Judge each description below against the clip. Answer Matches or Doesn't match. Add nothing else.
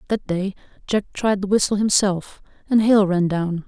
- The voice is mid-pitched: Doesn't match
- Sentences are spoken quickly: Doesn't match